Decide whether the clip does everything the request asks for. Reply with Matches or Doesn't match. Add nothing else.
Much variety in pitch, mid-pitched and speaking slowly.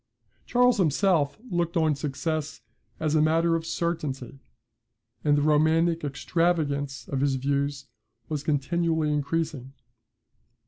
Doesn't match